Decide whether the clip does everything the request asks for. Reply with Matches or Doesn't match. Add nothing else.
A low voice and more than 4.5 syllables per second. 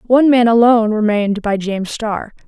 Doesn't match